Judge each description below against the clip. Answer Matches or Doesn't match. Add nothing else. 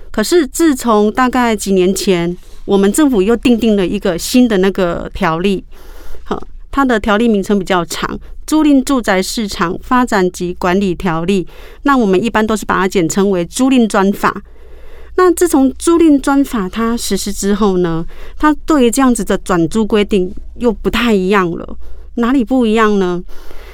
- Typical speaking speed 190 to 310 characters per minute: Matches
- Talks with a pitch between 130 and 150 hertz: Doesn't match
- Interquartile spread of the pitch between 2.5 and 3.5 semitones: Doesn't match